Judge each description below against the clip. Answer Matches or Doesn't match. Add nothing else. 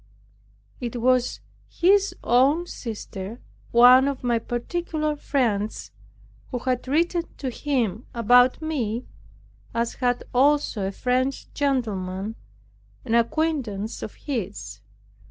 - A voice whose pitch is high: Matches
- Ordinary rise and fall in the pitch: Matches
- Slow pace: Matches